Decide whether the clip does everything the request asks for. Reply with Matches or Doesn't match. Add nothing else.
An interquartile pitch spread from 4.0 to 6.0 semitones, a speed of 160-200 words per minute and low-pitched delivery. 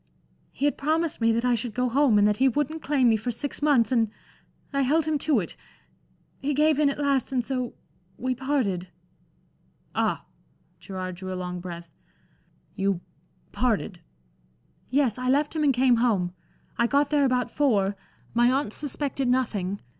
Doesn't match